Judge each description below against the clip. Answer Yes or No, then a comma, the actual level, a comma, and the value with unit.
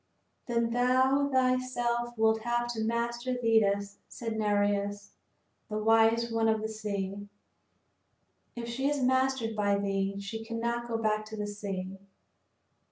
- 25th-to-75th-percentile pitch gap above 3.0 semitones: No, narrow, 2.6 semitones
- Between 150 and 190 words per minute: No, slow, 135 wpm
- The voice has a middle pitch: No, high, 225 Hz